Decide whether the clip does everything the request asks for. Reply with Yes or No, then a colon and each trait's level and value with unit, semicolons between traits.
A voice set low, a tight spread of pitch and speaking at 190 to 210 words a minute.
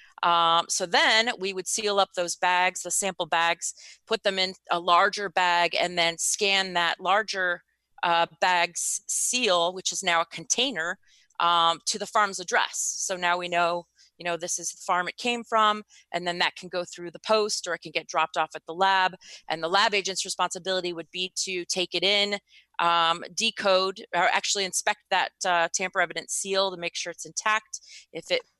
No: medium, 180 Hz; narrow, 2.3 semitones; average, 195 wpm